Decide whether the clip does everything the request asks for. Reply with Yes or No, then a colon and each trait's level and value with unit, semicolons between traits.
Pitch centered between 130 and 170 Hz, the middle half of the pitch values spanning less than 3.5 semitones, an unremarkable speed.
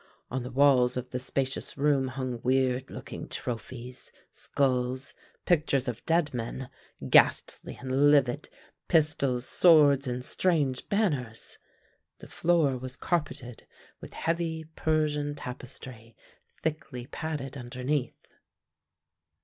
No: low, 135 Hz; average, 3.0 semitones; slow, 110 wpm